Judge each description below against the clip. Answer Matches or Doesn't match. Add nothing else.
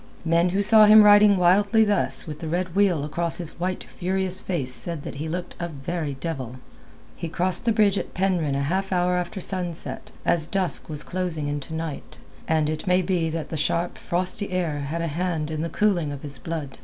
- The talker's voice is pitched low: Doesn't match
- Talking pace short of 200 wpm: Doesn't match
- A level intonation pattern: Doesn't match